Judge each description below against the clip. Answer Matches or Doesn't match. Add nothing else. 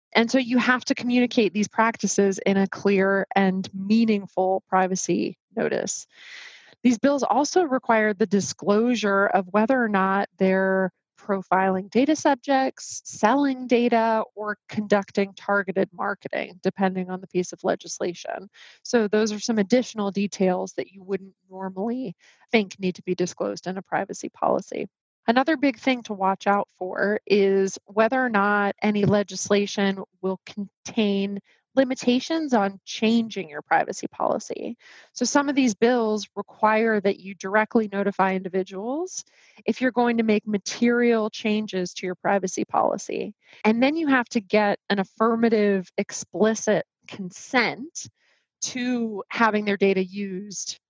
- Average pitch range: Matches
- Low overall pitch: Doesn't match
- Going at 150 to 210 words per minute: Doesn't match